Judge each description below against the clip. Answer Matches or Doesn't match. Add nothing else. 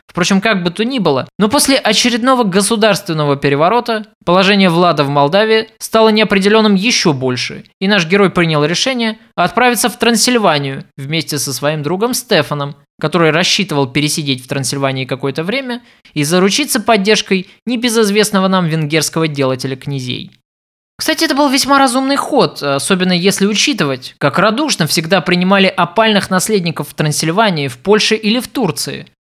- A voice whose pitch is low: Doesn't match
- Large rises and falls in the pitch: Matches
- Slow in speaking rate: Doesn't match